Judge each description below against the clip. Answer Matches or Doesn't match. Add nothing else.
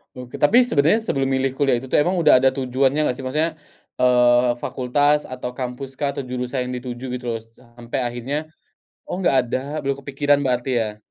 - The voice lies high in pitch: Doesn't match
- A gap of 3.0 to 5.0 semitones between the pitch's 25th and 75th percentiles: Doesn't match